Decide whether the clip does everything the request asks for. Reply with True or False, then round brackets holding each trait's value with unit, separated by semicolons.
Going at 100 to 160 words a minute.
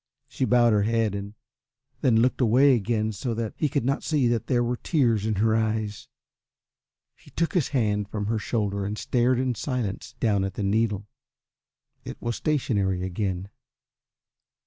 False (170 wpm)